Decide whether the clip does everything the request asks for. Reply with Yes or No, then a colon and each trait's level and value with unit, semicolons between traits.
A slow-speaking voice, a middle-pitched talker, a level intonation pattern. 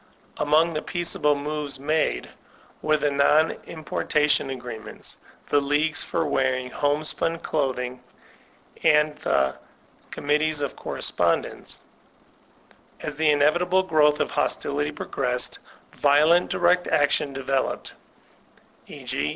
Yes: slow, 110 wpm; medium, 150 Hz; narrow, 2.0 semitones